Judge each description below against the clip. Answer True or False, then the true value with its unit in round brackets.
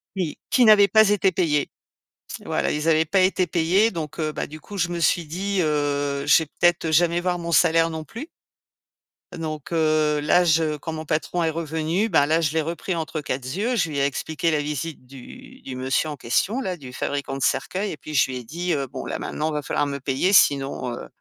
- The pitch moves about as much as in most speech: True (3.3 semitones)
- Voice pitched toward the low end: False (160 Hz)